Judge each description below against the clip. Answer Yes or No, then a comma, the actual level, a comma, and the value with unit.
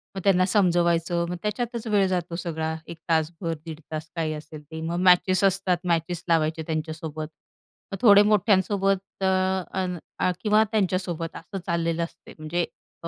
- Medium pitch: Yes, medium, 175 Hz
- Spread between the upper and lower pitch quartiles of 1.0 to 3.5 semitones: Yes, average, 2.8 semitones